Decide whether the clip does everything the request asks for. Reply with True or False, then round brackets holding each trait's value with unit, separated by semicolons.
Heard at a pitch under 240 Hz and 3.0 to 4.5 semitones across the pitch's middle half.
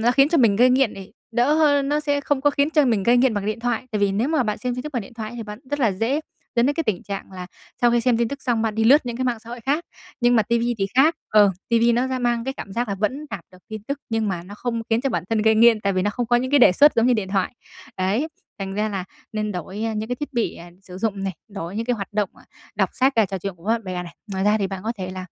True (225 Hz; 3.9 semitones)